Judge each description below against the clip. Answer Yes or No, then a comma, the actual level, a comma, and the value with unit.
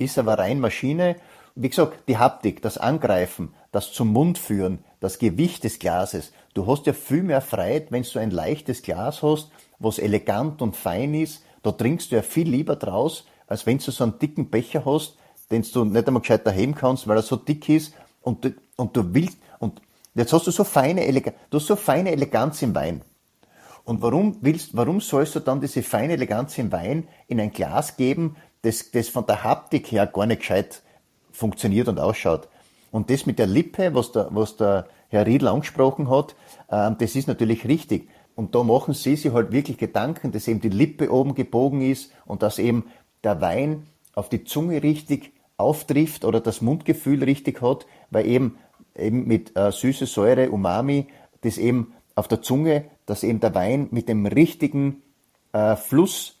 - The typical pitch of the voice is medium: No, low, 130 Hz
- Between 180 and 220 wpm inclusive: Yes, fast, 190 wpm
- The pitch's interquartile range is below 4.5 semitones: No, average, 4.9 semitones